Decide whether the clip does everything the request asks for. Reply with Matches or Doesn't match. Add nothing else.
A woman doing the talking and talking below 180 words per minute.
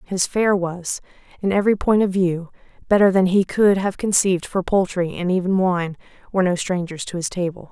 Doesn't match